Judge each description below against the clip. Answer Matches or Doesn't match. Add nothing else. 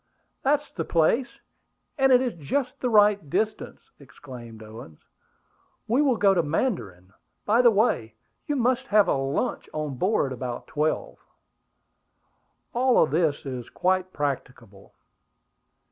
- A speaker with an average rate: Doesn't match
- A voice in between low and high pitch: Matches